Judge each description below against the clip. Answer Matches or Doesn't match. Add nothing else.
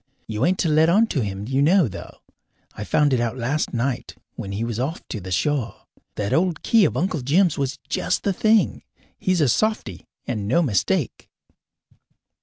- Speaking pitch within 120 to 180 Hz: Matches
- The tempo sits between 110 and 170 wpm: Doesn't match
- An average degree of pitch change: Doesn't match